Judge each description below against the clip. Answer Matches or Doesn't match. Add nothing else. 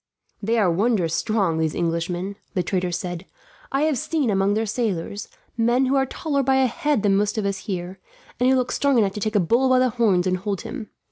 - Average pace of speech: Doesn't match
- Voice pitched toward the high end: Matches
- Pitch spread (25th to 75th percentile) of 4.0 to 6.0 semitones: Matches